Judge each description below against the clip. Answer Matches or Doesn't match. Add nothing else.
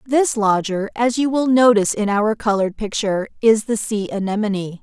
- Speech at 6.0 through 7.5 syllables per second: Doesn't match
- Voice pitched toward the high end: Matches